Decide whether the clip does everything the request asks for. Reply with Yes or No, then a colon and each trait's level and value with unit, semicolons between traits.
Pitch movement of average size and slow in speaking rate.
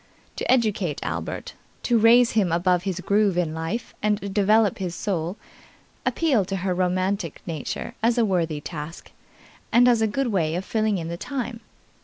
No: average, 4.3 semitones; average, 170 wpm